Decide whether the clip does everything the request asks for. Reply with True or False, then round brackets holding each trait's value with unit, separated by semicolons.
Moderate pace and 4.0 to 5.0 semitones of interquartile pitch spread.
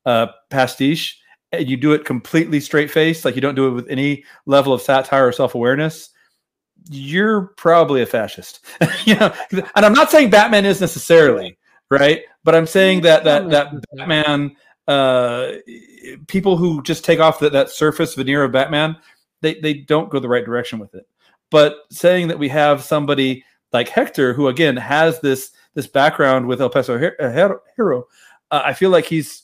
False (185 wpm; 3.3 semitones)